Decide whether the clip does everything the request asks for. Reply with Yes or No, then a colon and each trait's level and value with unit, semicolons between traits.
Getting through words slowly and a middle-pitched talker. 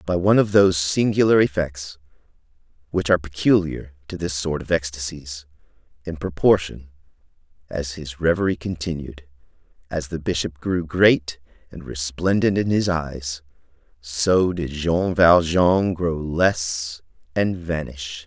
No: slow, 125 wpm; very low, 80 Hz